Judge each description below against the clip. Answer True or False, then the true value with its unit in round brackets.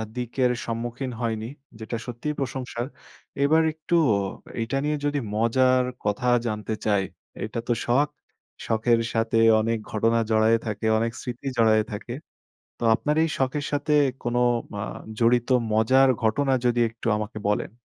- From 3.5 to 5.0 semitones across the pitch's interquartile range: False (2.9 semitones)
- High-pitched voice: False (120 Hz)